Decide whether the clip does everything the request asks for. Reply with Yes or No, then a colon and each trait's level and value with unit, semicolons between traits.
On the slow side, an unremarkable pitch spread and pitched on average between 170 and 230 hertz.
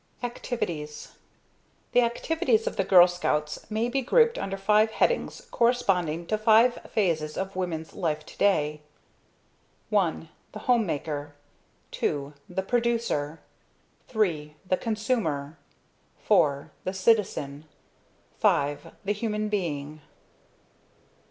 No: slow, 105 wpm; wide, 6.6 semitones; high, 190 Hz